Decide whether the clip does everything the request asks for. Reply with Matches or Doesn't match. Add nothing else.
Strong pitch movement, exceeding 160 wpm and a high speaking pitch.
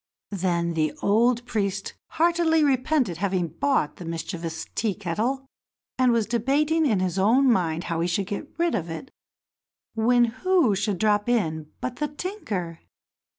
Doesn't match